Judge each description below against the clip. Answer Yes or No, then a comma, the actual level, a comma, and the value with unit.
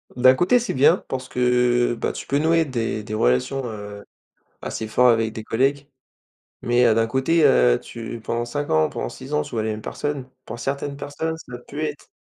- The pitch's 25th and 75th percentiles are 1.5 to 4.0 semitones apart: No, average, 4.4 semitones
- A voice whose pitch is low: Yes, low, 125 Hz